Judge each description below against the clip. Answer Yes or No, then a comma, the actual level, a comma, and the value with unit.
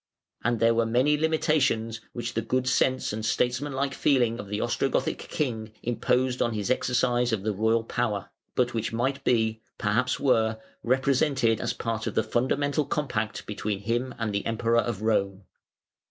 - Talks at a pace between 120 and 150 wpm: No, average, 165 wpm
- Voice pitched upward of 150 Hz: No, low, 120 Hz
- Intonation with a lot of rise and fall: No, narrow, 2.6 semitones